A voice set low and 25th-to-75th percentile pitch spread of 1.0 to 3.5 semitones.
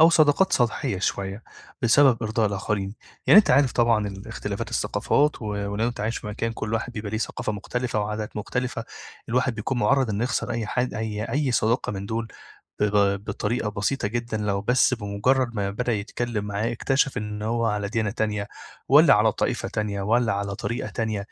Yes: low, 110 Hz; average, 2.8 semitones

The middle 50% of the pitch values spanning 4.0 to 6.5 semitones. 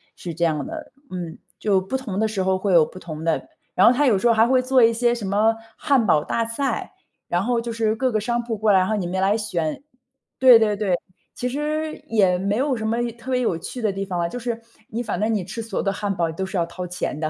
Yes: average, 4.3 semitones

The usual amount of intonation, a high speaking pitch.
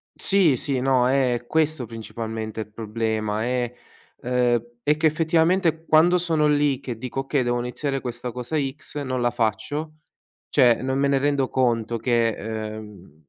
No: average, 4.1 semitones; low, 125 Hz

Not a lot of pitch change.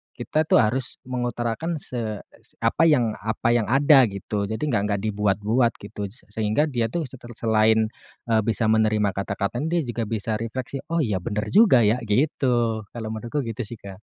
No: average, 3.0 semitones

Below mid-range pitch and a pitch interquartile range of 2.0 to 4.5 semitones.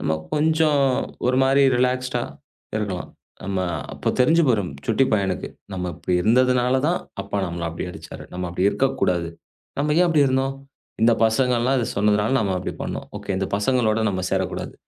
No: low, 120 Hz; wide, 5.4 semitones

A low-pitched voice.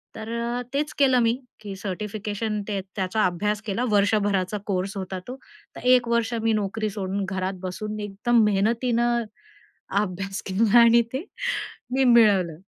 No: high, 210 Hz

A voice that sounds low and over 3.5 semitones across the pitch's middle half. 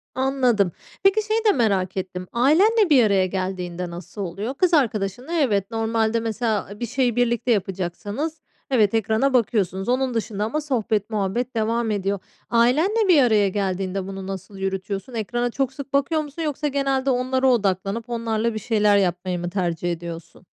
No: high, 225 Hz; average, 5.2 semitones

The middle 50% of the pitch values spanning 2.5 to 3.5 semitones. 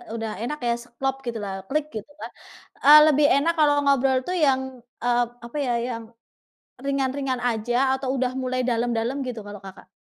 Yes: average, 2.9 semitones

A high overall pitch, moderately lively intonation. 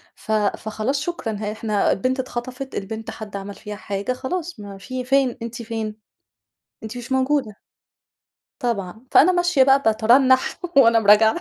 Yes: high, 230 Hz; average, 3.6 semitones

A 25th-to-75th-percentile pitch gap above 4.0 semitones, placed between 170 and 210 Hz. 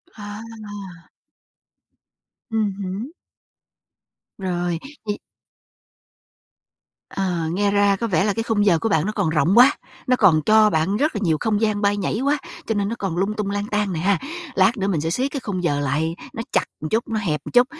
No: average, 3.6 semitones; high, 200 Hz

